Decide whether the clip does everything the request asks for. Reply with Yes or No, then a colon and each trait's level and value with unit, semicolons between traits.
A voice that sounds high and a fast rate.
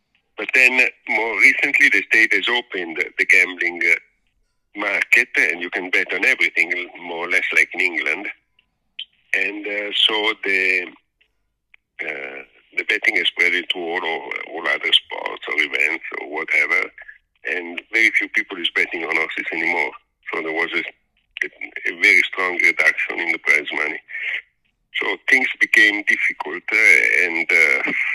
No: very high, 390 Hz; average, 145 wpm